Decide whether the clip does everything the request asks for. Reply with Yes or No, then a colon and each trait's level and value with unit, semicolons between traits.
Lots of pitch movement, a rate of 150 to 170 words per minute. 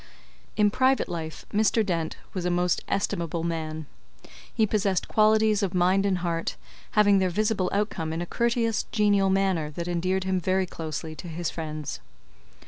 No: average, 3.6 semitones; average, 160 wpm